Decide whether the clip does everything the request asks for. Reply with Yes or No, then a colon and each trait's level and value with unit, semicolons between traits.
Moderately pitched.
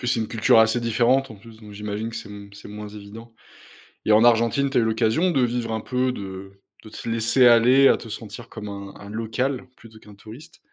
No: low, 115 Hz